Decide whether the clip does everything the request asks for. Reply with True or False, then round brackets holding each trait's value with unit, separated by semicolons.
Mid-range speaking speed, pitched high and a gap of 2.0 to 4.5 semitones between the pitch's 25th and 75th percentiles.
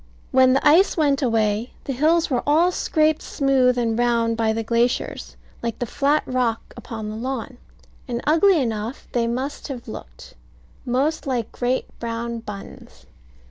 True (155 wpm; 250 Hz; 3.4 semitones)